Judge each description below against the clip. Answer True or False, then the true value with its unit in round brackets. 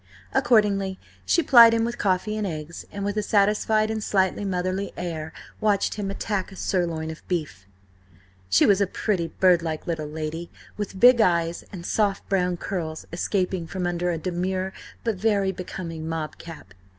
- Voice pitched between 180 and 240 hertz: True (185 Hz)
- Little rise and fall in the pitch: False (3.3 semitones)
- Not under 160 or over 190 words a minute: True (165 wpm)